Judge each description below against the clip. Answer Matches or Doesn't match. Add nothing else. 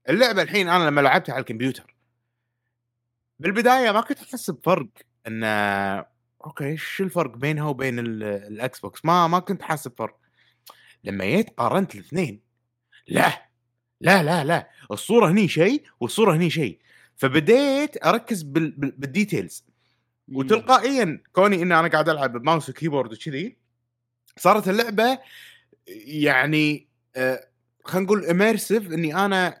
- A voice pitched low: Doesn't match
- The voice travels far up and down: Matches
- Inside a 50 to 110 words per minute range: Doesn't match